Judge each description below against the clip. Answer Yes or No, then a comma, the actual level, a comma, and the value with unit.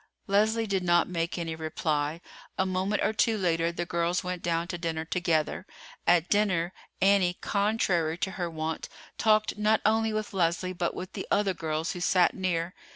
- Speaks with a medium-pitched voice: Yes, medium, 180 Hz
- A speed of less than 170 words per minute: No, average, 175 wpm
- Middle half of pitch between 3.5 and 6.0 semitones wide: No, average, 3.1 semitones